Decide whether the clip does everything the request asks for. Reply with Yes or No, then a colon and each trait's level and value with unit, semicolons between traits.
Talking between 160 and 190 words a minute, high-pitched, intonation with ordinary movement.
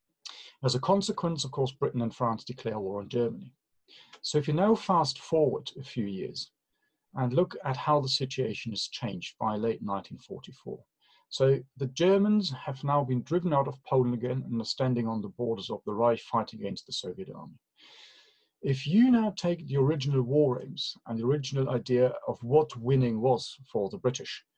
No: average, 185 wpm; low, 135 Hz; average, 3.7 semitones